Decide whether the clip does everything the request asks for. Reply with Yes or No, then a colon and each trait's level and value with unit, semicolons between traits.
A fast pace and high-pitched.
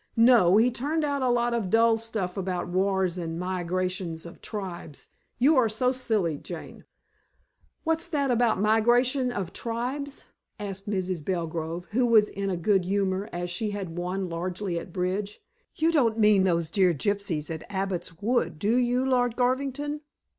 No: average, 160 wpm; high, 205 Hz